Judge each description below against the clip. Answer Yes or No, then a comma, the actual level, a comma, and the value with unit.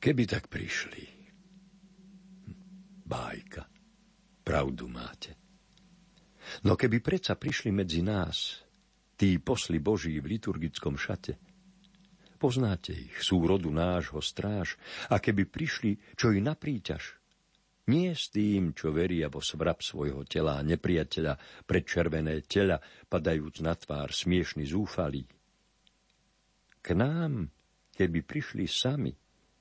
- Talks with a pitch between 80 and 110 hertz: Yes, low, 100 Hz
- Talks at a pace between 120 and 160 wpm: No, slow, 110 wpm